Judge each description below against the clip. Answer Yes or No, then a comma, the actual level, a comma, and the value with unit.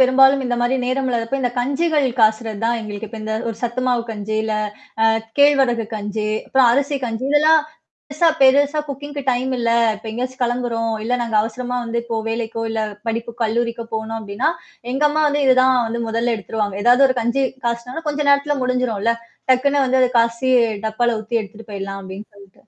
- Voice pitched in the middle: No, high, 240 Hz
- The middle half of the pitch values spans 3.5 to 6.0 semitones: No, average, 2.9 semitones